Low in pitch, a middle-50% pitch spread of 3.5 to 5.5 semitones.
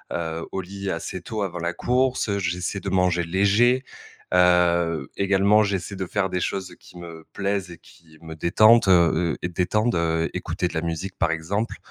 No: very low, 90 Hz; average, 2.9 semitones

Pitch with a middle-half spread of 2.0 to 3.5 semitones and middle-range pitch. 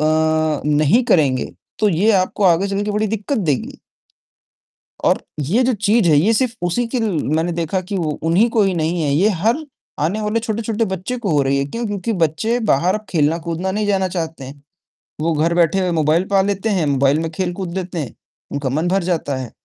No: average, 4.8 semitones; medium, 175 Hz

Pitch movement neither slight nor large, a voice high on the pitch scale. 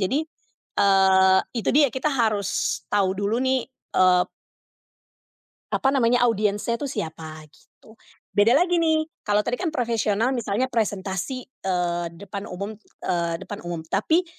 Yes: average, 5.0 semitones; high, 210 Hz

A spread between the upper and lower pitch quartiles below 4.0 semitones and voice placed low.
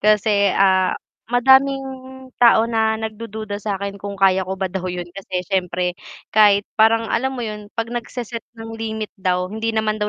No: average, 2.7 semitones; high, 215 Hz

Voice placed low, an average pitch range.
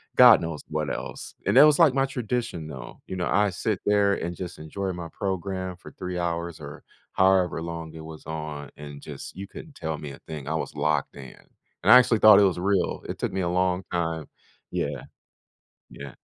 Yes: very low, 90 Hz; average, 3.9 semitones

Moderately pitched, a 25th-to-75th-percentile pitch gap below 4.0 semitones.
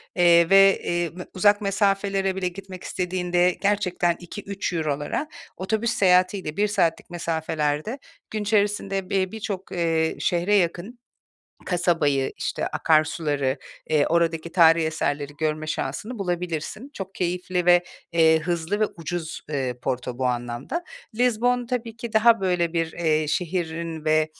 Yes: medium, 175 Hz; average, 3.6 semitones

